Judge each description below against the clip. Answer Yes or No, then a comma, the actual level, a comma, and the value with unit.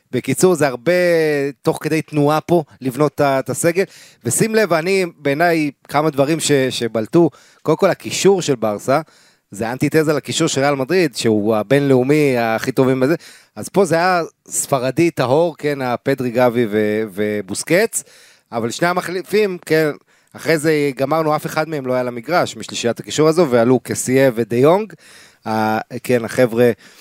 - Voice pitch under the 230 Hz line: Yes, medium, 140 Hz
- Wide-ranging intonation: No, average, 4.9 semitones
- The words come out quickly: Yes, fast, 155 wpm